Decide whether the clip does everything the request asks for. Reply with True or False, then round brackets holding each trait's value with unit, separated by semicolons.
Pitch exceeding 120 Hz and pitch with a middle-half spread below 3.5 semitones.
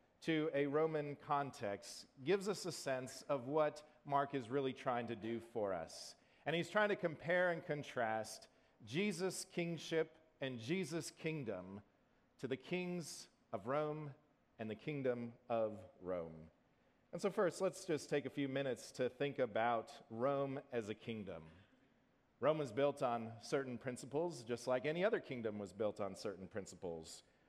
False (140 Hz; 5.5 semitones)